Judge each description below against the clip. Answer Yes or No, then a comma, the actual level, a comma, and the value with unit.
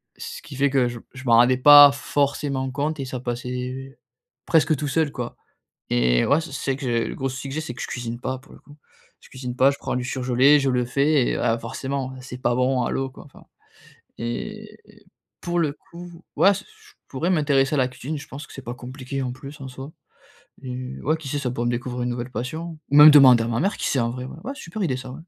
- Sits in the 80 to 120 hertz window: No, low, 135 Hz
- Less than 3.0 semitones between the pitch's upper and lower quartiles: Yes, narrow, 2.6 semitones